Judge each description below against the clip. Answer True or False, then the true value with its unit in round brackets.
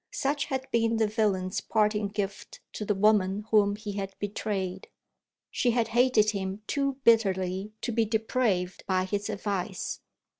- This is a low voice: False (210 Hz)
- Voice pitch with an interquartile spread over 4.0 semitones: False (2.5 semitones)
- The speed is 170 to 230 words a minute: False (150 wpm)